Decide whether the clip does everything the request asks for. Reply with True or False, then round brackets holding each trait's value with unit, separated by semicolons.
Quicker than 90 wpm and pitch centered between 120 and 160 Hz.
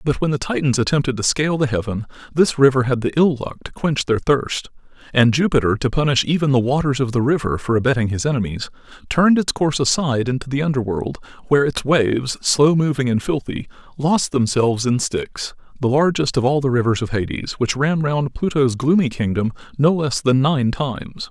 True (200 wpm; 135 Hz)